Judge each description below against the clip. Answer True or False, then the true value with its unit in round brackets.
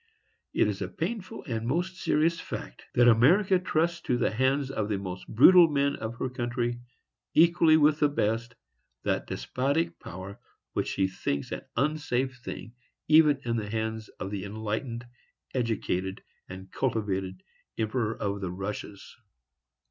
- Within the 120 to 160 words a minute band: True (150 wpm)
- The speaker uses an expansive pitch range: True (6.0 semitones)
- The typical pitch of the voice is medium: False (120 Hz)